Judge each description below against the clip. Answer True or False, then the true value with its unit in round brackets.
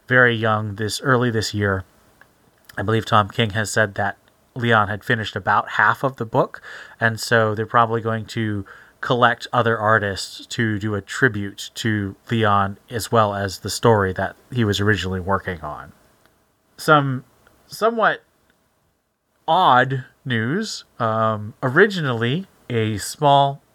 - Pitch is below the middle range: True (110 Hz)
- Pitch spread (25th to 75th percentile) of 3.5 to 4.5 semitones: False (3.0 semitones)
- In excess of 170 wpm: False (140 wpm)